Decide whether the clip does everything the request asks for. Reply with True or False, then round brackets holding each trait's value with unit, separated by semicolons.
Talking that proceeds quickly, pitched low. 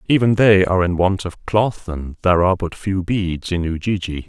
True (210 wpm; 95 Hz)